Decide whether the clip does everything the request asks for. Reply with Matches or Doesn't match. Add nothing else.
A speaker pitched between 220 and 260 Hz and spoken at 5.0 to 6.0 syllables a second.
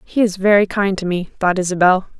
Doesn't match